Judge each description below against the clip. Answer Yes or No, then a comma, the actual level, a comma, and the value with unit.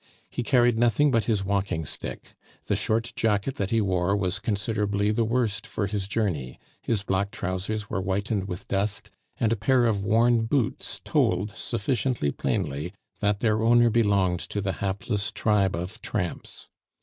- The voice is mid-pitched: No, low, 105 Hz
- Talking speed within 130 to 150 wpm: No, average, 160 wpm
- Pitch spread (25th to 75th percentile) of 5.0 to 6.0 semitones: No, average, 2.7 semitones